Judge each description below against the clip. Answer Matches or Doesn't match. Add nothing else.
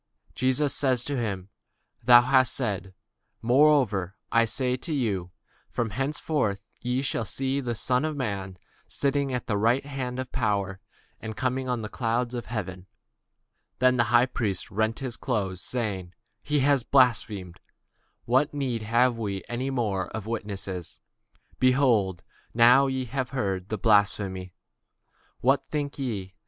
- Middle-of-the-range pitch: Doesn't match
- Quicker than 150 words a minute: Doesn't match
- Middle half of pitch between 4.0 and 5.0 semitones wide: Matches